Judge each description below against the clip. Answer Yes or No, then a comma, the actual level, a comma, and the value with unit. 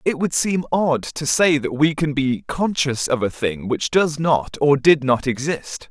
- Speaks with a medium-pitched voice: Yes, medium, 145 Hz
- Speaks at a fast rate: Yes, fast, 215 wpm